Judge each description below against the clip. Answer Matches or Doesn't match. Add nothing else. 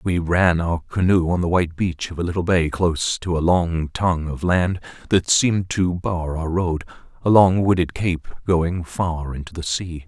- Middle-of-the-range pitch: Doesn't match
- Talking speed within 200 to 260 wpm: Matches